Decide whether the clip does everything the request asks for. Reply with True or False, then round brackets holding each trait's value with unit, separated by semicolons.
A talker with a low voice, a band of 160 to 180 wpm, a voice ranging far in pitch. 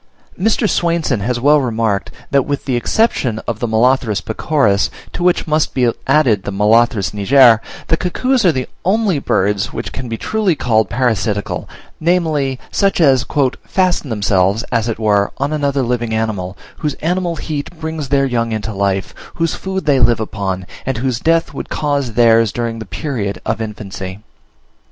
True (120 Hz; 165 wpm; 5.8 semitones)